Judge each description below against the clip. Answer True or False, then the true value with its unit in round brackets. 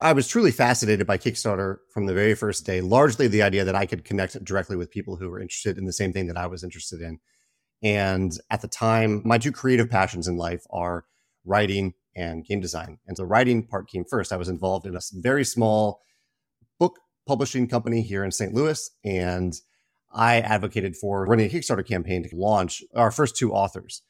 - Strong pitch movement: False (4.0 semitones)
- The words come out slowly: False (205 wpm)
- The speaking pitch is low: True (100 Hz)